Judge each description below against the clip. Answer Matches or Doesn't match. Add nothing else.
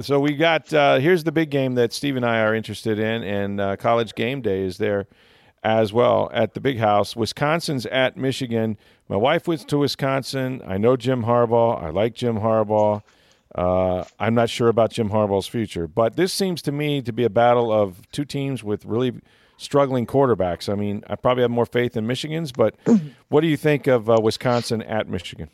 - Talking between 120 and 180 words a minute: Doesn't match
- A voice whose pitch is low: Matches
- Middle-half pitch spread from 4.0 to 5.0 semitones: Matches